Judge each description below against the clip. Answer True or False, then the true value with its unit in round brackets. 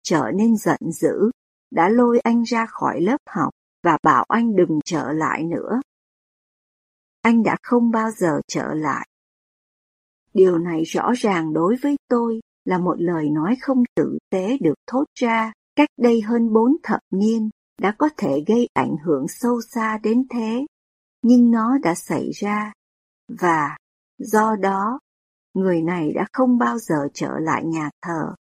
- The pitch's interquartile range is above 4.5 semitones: True (5.2 semitones)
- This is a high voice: True (220 Hz)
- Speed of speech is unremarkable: False (160 wpm)